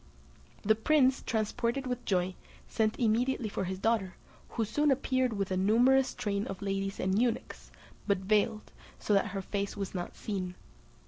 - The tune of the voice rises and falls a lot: No, average, 3.8 semitones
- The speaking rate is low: No, average, 165 wpm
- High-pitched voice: Yes, high, 215 Hz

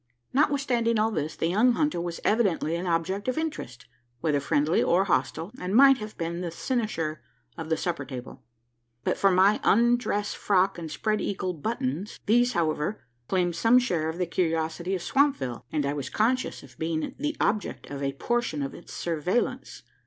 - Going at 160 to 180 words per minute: Yes, average, 175 wpm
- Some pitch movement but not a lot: No, wide, 6.4 semitones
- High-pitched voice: No, medium, 180 Hz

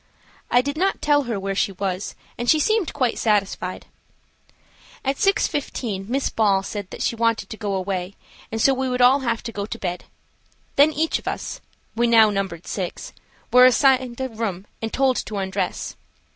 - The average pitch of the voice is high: Yes, high, 230 Hz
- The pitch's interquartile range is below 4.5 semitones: No, average, 5.1 semitones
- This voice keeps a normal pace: Yes, average, 175 wpm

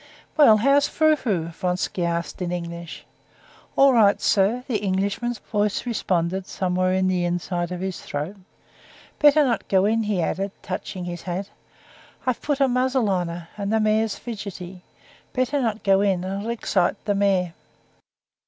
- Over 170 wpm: No, average, 160 wpm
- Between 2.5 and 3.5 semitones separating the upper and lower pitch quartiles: No, average, 4.0 semitones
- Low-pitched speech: No, high, 195 Hz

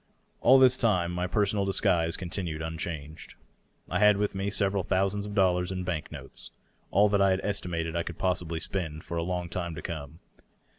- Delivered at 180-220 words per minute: Yes, average, 200 wpm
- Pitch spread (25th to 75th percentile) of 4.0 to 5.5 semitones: No, average, 3.0 semitones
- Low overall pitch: Yes, very low, 90 Hz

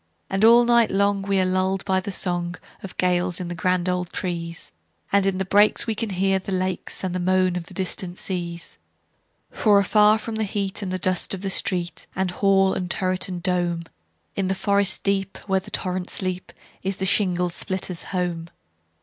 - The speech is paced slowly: No, average, 165 wpm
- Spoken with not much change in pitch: Yes, narrow, 1.6 semitones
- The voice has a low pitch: No, medium, 185 Hz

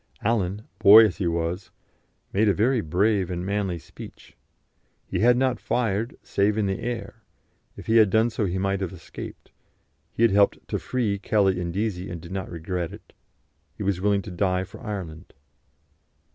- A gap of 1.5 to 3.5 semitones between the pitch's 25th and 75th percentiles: Yes, average, 3.2 semitones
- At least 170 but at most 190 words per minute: Yes, average, 180 wpm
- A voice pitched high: No, low, 100 Hz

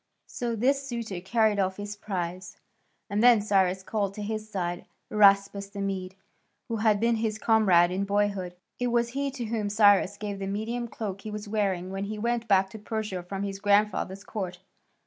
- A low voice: No, high, 205 Hz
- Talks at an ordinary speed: Yes, average, 185 wpm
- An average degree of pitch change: No, narrow, 2.2 semitones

